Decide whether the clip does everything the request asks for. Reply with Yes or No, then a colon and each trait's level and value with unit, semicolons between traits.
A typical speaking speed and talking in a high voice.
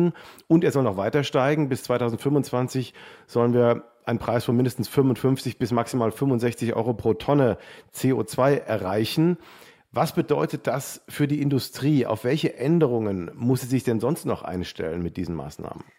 No: average, 160 wpm; low, 125 Hz